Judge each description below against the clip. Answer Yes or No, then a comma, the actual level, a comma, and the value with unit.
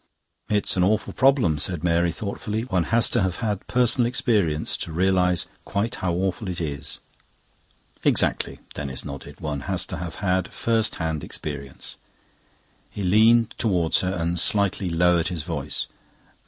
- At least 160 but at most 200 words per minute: No, average, 150 wpm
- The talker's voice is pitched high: No, very low, 90 Hz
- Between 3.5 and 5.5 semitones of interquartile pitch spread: Yes, average, 4.2 semitones